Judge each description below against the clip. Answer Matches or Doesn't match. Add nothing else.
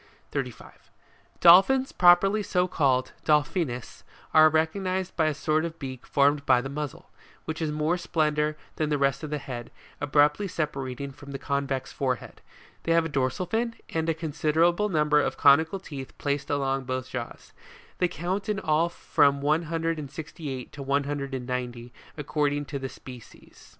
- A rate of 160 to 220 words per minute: Matches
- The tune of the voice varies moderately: Matches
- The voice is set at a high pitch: Doesn't match